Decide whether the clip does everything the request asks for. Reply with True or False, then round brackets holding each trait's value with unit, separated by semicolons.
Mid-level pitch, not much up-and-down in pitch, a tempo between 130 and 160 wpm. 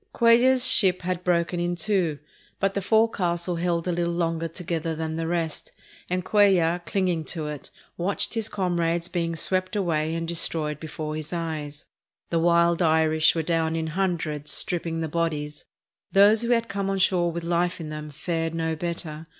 False (170 Hz; 2.1 semitones; 175 wpm)